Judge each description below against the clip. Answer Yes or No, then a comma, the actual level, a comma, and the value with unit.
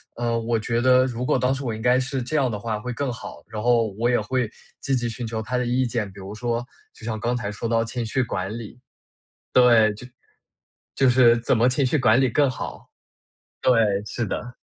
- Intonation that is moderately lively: No, narrow, 2.2 semitones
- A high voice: No, low, 120 Hz